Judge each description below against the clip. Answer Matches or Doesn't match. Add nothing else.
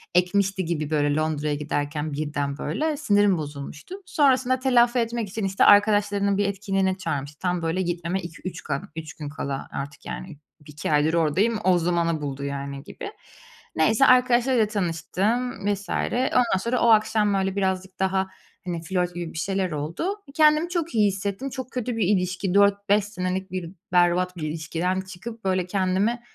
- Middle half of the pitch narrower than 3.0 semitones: Doesn't match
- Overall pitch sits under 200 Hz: Matches